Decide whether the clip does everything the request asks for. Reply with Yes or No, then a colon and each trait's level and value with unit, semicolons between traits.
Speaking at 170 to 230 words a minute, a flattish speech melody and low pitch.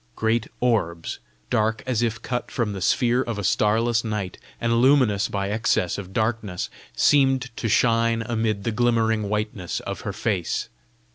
No: average, 155 wpm; narrow, 2.2 semitones; low, 110 Hz